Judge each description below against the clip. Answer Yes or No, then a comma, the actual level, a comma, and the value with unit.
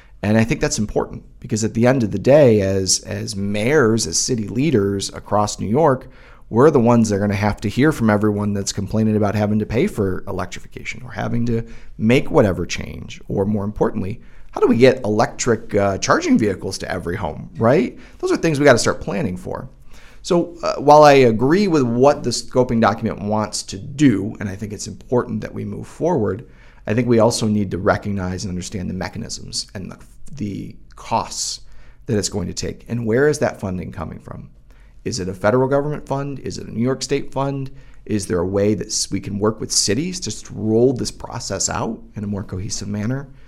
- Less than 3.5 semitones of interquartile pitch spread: No, average, 4.0 semitones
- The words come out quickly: Yes, fast, 210 wpm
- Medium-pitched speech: No, low, 110 Hz